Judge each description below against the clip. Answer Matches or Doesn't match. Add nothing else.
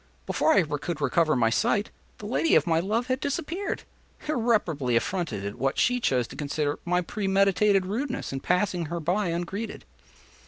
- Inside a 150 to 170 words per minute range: Matches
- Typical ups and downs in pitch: Doesn't match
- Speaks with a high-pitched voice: Doesn't match